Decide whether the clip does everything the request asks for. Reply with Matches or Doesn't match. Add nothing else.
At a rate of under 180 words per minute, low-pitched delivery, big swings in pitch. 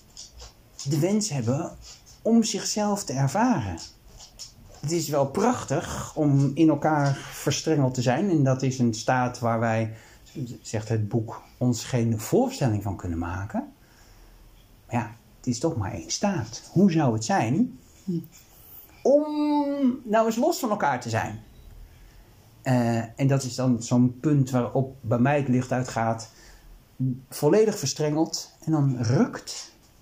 Matches